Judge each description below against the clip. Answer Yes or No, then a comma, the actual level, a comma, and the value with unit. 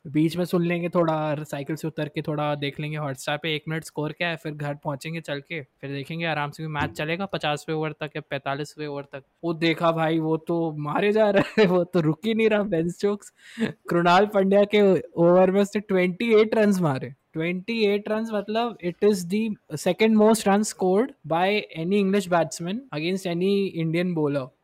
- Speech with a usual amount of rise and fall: Yes, average, 4.7 semitones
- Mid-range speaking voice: Yes, medium, 170 Hz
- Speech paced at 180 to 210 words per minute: Yes, fast, 190 wpm